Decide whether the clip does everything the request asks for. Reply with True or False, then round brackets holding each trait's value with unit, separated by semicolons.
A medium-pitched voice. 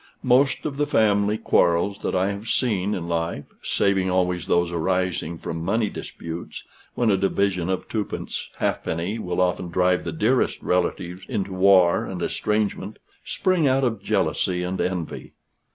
False (95 Hz)